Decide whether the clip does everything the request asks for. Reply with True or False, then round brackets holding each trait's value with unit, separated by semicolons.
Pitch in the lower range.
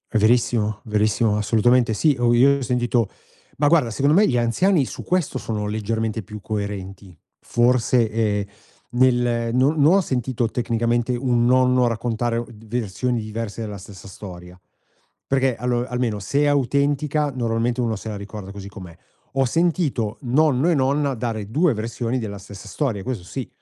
True (120 Hz)